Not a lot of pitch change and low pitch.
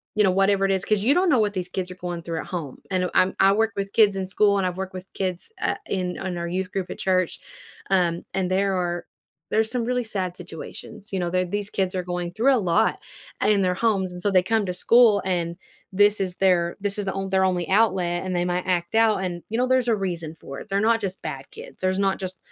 No: narrow, 2.3 semitones; high, 190 Hz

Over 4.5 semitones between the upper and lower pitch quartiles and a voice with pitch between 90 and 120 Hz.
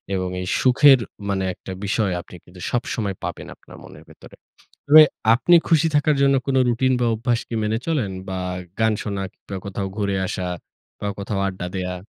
Yes: average, 5.3 semitones; low, 110 Hz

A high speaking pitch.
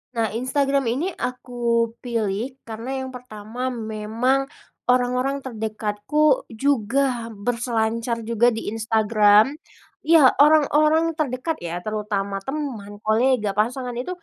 Yes: high, 240 Hz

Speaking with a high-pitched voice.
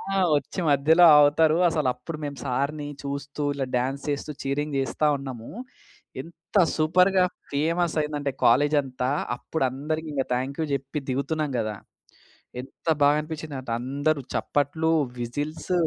No: medium, 145 Hz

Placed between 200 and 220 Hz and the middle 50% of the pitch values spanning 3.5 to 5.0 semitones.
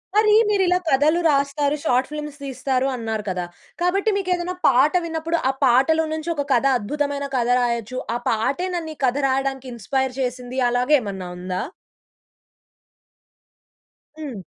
No: very high, 270 Hz; average, 4.3 semitones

